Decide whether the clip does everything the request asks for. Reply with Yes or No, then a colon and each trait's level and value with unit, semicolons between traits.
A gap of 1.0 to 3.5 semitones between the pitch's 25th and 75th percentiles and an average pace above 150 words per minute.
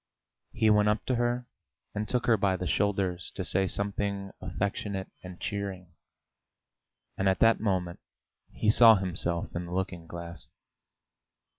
No: narrow, 2.6 semitones; average, 145 wpm